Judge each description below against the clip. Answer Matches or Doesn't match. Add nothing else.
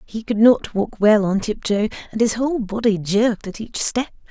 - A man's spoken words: Doesn't match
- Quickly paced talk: Matches